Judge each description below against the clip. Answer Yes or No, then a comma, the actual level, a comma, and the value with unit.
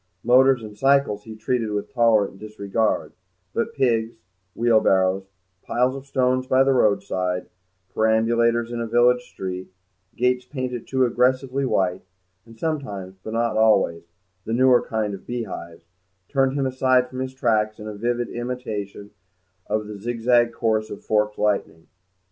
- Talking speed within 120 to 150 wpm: Yes, average, 145 wpm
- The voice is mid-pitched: No, low, 115 Hz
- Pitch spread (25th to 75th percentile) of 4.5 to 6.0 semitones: No, average, 3.2 semitones